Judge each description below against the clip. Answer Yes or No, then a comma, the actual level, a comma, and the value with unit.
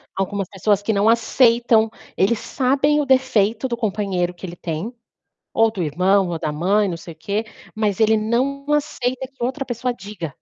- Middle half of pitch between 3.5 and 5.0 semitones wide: Yes, average, 4.3 semitones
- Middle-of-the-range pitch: No, high, 215 Hz